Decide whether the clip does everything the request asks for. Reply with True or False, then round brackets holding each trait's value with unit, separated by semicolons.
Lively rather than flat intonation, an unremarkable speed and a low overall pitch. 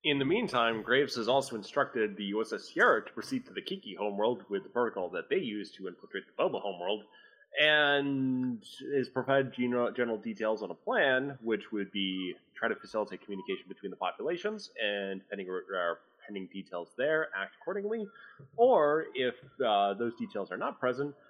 True (6.1 semitones; 170 wpm; 130 Hz)